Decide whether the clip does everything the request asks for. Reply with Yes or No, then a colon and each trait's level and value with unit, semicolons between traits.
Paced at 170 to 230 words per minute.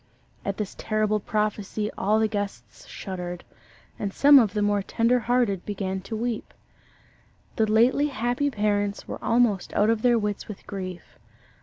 No: average, 155 wpm